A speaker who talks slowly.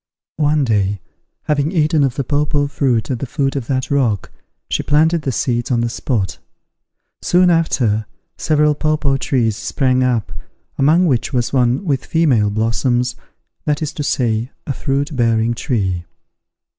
No: average, 155 wpm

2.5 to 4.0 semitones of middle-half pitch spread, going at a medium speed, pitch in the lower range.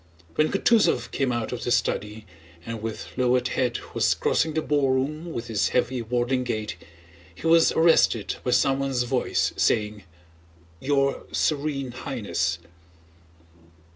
No: average, 3.7 semitones; slow, 130 wpm; low, 125 Hz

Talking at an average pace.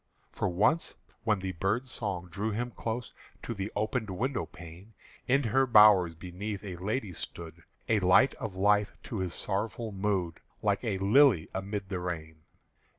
Yes: average, 160 wpm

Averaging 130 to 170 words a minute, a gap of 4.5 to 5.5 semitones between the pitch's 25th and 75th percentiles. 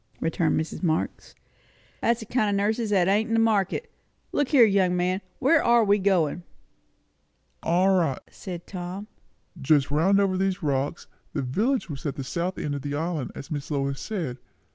No: average, 180 wpm; average, 5.1 semitones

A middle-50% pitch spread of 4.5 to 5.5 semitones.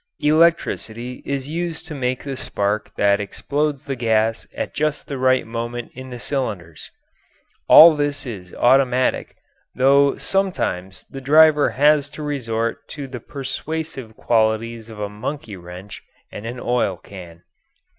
Yes: average, 4.8 semitones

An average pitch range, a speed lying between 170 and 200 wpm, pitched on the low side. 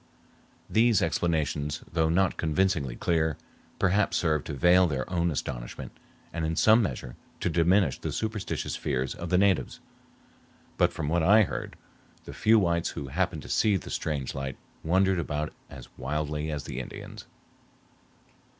No: average, 4.0 semitones; average, 150 wpm; very low, 80 Hz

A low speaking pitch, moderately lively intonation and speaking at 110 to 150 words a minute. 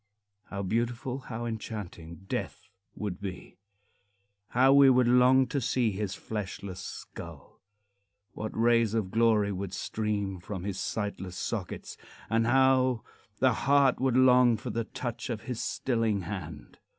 Yes: low, 115 Hz; average, 3.9 semitones; average, 140 wpm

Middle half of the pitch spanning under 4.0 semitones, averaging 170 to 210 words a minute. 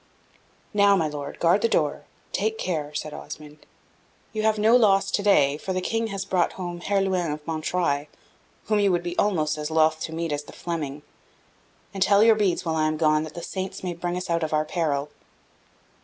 No: average, 4.3 semitones; fast, 205 wpm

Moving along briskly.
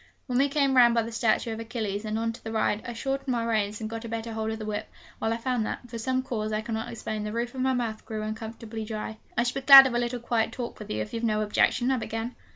Yes: fast, 290 wpm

